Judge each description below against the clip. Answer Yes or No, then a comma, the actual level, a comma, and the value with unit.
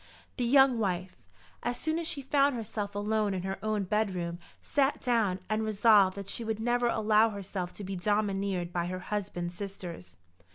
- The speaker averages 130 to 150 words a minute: No, average, 175 wpm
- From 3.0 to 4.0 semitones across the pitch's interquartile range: Yes, average, 3.3 semitones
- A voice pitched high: Yes, high, 205 Hz